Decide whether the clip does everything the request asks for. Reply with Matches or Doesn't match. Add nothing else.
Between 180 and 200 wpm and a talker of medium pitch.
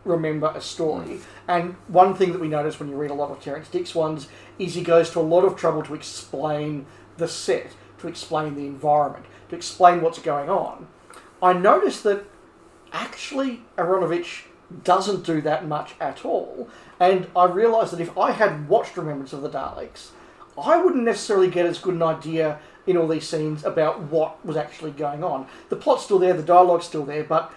Matches